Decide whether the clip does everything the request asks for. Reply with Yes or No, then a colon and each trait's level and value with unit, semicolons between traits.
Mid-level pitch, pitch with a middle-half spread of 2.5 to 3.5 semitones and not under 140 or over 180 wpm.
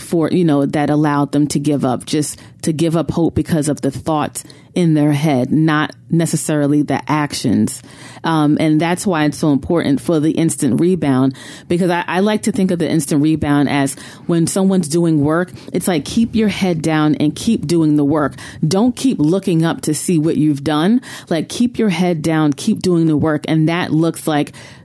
No: medium, 155 Hz; average, 2.8 semitones; fast, 205 wpm